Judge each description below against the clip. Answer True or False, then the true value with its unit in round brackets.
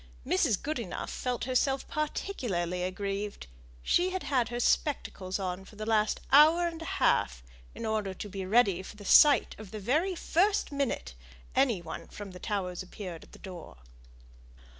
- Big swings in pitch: True (6.9 semitones)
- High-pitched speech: True (215 Hz)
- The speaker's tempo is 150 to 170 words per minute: True (160 wpm)